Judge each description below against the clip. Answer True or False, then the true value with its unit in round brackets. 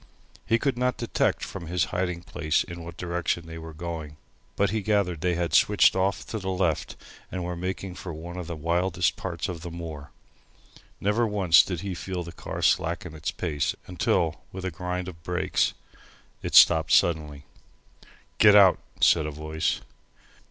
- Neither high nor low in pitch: False (85 Hz)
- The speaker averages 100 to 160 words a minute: False (175 wpm)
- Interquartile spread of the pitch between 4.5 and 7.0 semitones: False (2.4 semitones)